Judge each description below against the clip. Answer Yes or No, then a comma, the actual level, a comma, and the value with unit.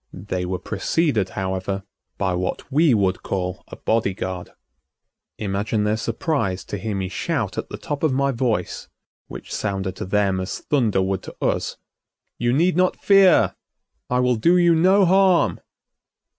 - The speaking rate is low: No, average, 160 wpm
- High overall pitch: No, low, 105 Hz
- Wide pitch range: Yes, wide, 7.6 semitones